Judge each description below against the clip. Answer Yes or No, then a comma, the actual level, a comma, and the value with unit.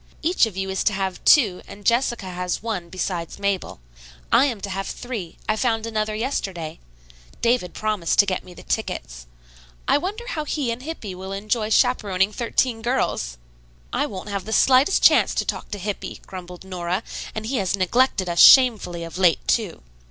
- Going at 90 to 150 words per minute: No, average, 180 wpm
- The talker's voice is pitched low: No, high, 205 Hz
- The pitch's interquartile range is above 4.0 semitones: Yes, average, 4.4 semitones